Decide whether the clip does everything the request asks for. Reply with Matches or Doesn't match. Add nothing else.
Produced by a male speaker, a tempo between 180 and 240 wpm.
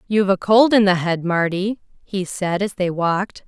Doesn't match